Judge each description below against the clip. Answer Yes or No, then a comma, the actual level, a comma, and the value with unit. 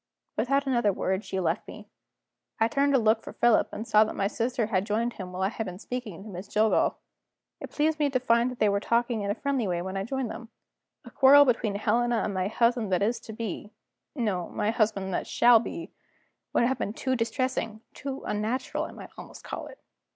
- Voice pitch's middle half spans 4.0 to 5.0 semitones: No, average, 3.4 semitones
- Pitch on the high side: Yes, high, 225 Hz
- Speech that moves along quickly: Yes, fast, 220 wpm